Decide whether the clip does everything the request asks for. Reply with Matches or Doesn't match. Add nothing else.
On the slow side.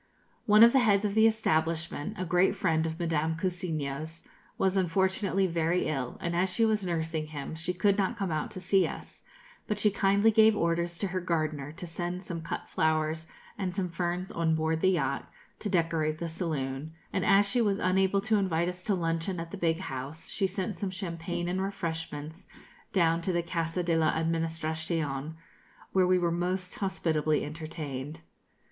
Doesn't match